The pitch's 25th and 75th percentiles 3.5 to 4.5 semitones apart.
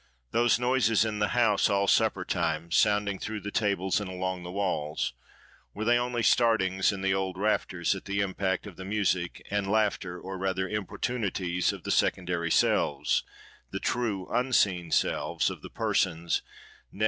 No: average, 2.7 semitones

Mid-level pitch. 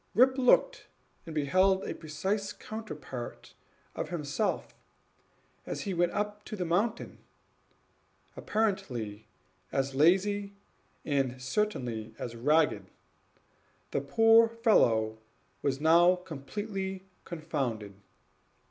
Yes: medium, 175 Hz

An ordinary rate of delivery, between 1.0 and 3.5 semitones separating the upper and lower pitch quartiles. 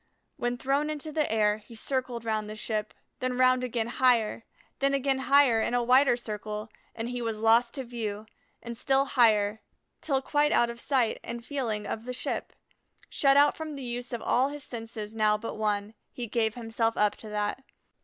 Yes: average, 195 wpm; average, 3.2 semitones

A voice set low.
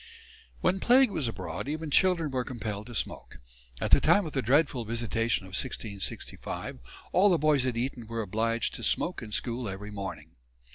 Yes: low, 120 Hz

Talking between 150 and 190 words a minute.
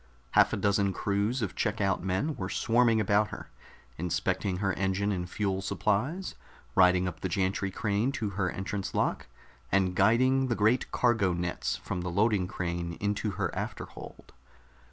Yes: average, 160 wpm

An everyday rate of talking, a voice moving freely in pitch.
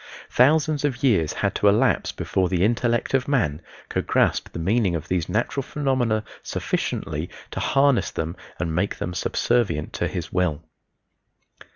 Yes: average, 155 wpm; wide, 6.9 semitones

